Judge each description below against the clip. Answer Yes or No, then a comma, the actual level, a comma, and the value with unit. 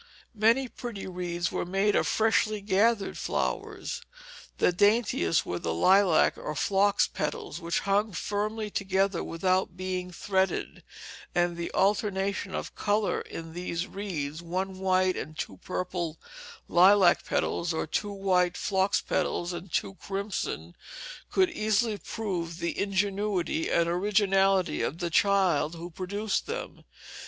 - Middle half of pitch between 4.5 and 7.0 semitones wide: No, average, 2.8 semitones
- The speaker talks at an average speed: No, slow, 130 wpm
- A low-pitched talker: No, high, 190 Hz